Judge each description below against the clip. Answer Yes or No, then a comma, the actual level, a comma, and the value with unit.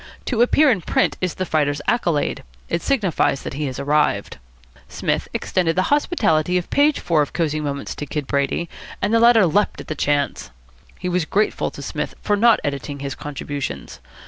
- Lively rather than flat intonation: Yes, wide, 6.2 semitones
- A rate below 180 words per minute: No, average, 185 wpm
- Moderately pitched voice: Yes, medium, 165 Hz